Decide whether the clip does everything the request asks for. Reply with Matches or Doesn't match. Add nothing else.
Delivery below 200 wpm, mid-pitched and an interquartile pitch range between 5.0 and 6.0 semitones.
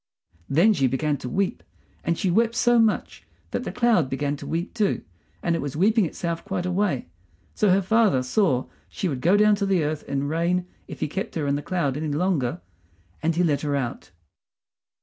Doesn't match